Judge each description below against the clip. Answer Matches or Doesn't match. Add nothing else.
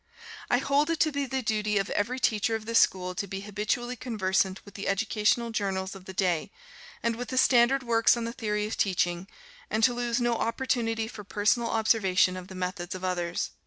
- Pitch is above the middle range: Matches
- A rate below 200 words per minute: Doesn't match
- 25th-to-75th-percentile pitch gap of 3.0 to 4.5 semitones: Matches